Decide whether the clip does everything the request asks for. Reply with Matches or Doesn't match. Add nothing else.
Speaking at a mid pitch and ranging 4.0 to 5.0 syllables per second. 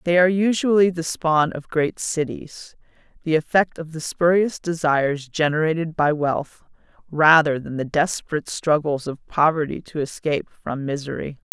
Matches